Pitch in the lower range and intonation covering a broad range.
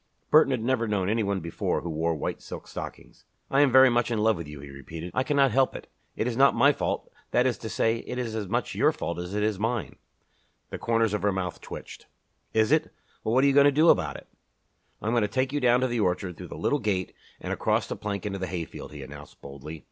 Yes: low, 110 Hz; wide, 6.0 semitones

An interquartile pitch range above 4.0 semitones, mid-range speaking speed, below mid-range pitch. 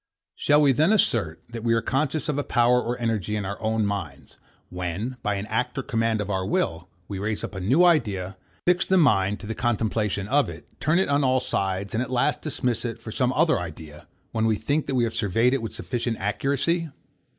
No: average, 4.9 semitones; fast, 225 wpm; low, 115 Hz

